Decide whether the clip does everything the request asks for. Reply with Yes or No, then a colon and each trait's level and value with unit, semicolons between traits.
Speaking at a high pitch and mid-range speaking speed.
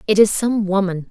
No: high, 200 Hz; fast, 215 wpm